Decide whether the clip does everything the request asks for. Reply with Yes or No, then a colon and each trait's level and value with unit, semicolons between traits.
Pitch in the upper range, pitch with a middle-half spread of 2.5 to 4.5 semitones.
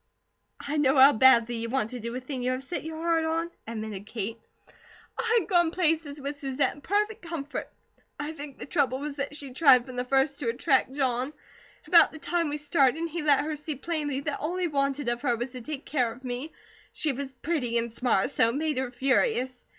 Yes: very high, 280 Hz; average, 3.7 semitones